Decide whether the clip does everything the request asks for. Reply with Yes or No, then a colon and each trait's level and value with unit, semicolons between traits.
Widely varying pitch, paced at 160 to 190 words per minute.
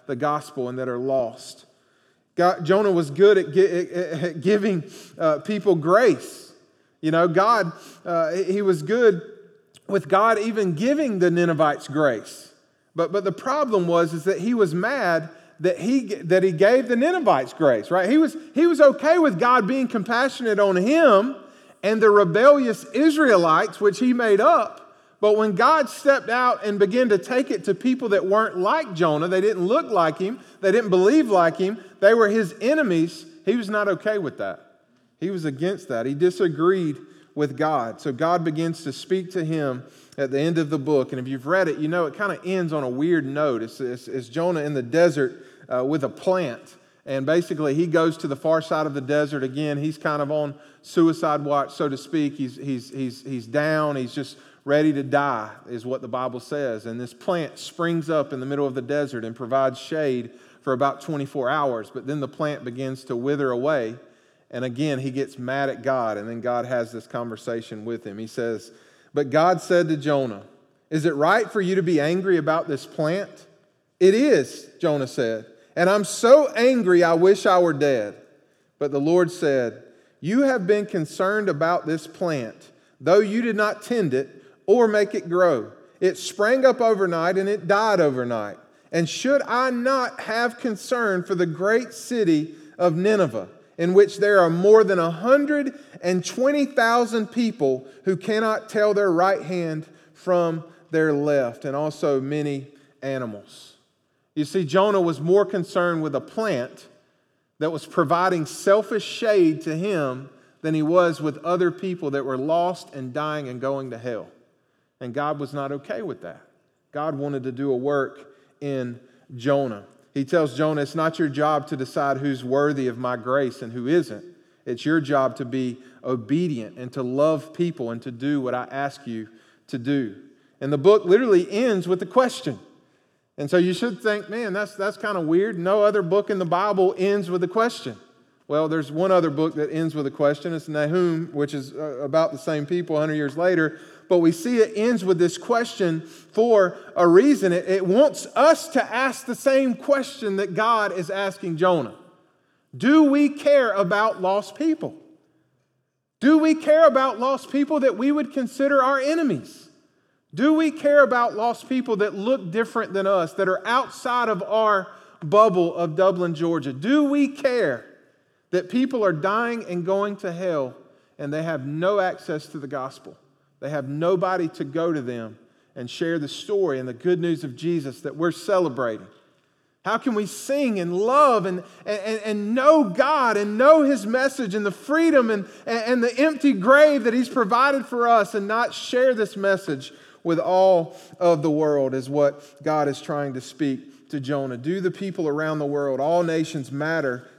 Yes: wide, 6.5 semitones; average, 185 wpm